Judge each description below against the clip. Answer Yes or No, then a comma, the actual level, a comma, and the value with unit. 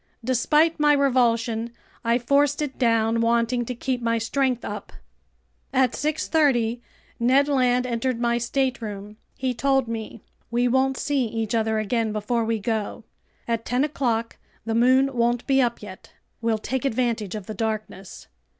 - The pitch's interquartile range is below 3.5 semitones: Yes, average, 2.7 semitones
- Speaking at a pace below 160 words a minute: Yes, average, 150 wpm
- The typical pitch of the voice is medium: No, high, 235 Hz